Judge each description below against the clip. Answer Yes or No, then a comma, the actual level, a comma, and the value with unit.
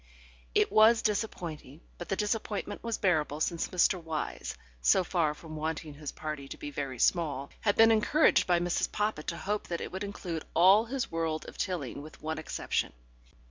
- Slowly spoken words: No, average, 180 wpm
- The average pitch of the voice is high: No, medium, 170 Hz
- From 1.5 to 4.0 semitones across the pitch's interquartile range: No, average, 4.9 semitones